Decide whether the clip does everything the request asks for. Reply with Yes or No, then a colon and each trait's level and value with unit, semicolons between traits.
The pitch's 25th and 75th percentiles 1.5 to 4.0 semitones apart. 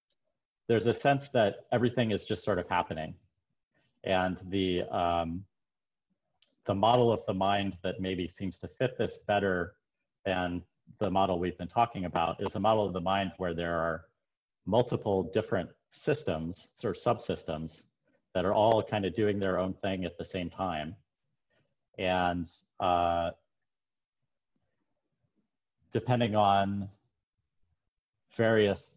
Yes: average, 3.2 semitones